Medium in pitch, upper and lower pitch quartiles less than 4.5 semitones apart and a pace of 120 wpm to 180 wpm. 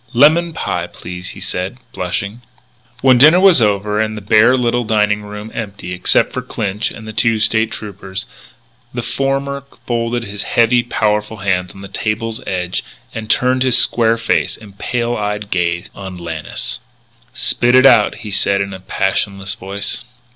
No: low, 110 Hz; average, 3.4 semitones; average, 165 wpm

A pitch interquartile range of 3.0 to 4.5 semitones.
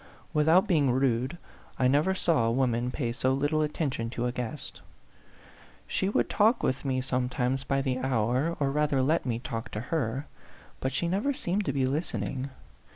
Yes: average, 3.7 semitones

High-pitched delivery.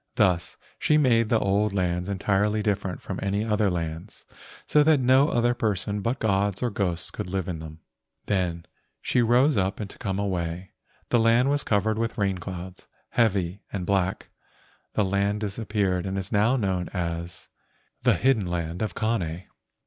No: low, 100 Hz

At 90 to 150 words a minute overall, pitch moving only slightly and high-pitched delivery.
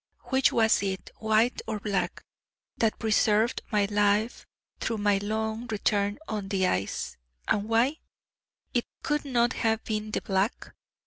Yes: average, 140 wpm; narrow, 1.8 semitones; high, 215 Hz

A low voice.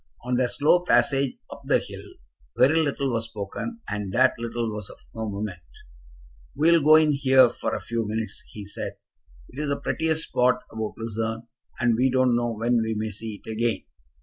Yes: low, 120 Hz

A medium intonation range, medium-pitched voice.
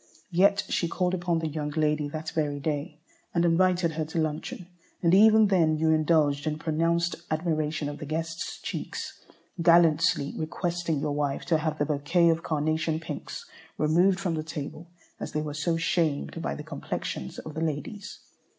No: narrow, 1.9 semitones; medium, 160 Hz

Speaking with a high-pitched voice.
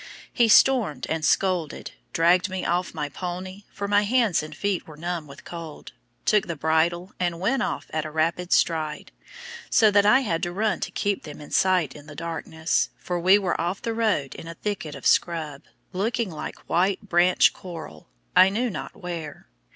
No: medium, 175 Hz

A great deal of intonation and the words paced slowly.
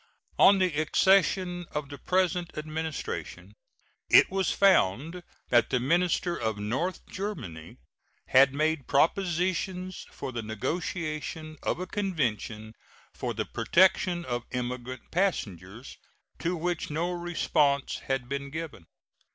Yes: wide, 5.9 semitones; slow, 120 wpm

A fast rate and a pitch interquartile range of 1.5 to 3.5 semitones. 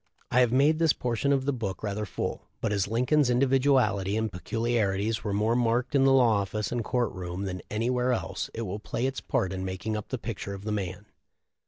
No: fast, 215 wpm; average, 3.9 semitones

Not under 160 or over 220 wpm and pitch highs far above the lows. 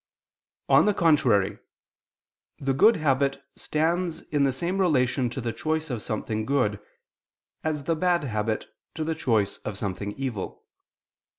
No: average, 140 wpm; wide, 6.3 semitones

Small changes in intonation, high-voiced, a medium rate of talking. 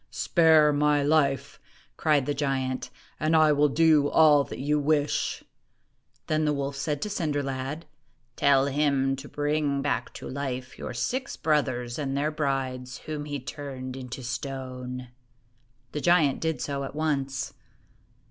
No: narrow, 2.2 semitones; medium, 140 Hz; average, 155 wpm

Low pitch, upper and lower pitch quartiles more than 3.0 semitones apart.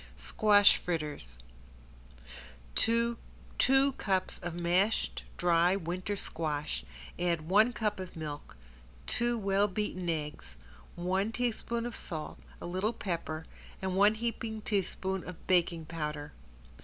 No: medium, 185 Hz; average, 4.4 semitones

